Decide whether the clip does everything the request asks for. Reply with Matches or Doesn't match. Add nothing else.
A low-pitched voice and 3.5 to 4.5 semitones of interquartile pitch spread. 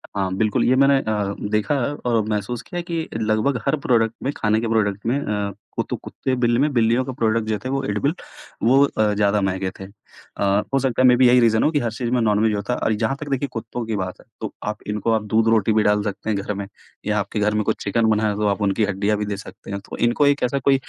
Doesn't match